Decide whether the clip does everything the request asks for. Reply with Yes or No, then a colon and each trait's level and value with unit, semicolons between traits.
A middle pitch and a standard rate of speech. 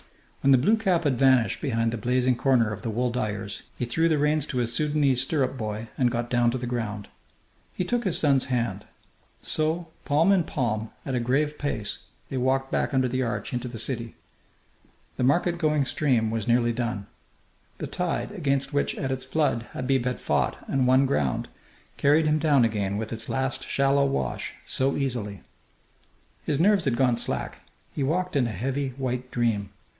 No: low, 130 Hz; average, 190 wpm